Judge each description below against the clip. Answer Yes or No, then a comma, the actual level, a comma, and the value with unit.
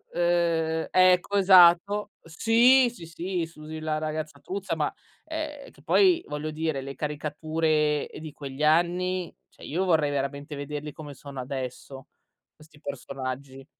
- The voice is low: No, medium, 155 Hz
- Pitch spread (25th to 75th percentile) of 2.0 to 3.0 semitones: No, average, 3.7 semitones